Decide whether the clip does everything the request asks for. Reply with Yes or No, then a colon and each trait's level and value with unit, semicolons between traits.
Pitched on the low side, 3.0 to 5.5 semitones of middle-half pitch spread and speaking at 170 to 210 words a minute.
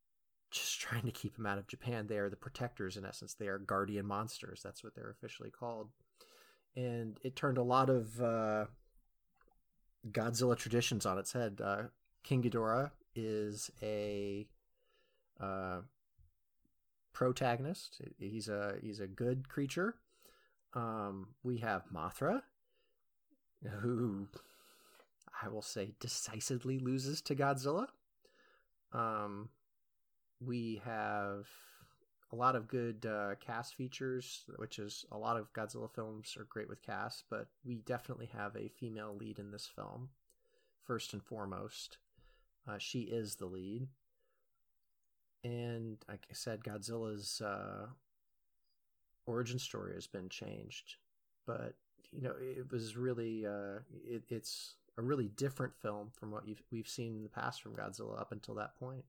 No: low, 115 Hz; average, 3.5 semitones; average, 140 wpm